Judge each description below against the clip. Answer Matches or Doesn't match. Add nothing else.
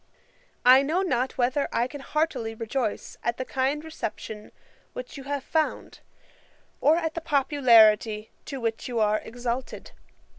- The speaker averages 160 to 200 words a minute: Doesn't match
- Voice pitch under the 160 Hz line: Doesn't match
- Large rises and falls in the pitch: Doesn't match